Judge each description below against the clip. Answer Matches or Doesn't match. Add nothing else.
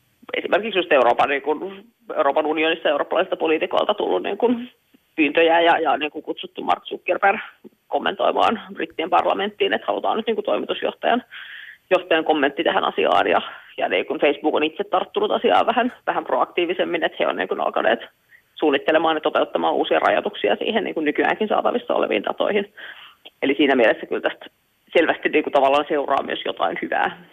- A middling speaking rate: Doesn't match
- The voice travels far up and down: Matches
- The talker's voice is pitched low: Doesn't match